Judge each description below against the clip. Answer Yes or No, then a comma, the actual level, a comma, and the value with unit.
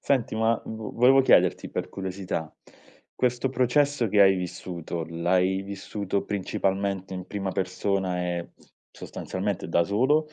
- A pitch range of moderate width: Yes, average, 3.6 semitones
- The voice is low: Yes, low, 100 Hz